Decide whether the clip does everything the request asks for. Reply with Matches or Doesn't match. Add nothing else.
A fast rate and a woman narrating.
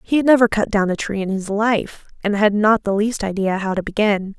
Matches